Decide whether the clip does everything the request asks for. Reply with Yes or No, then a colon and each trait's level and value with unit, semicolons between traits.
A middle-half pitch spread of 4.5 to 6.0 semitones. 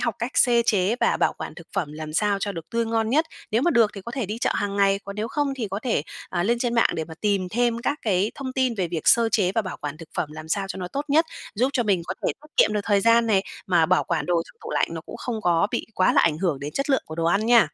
Yes: average, 4.8 semitones